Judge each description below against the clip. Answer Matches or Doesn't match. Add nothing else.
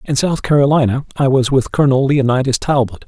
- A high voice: Doesn't match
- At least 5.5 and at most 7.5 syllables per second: Matches